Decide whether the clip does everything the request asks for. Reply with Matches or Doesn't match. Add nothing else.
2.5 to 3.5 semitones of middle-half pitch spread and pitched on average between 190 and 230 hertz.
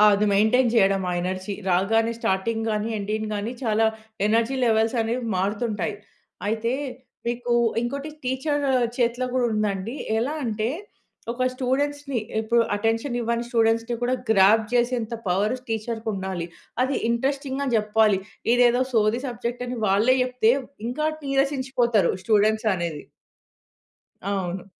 Matches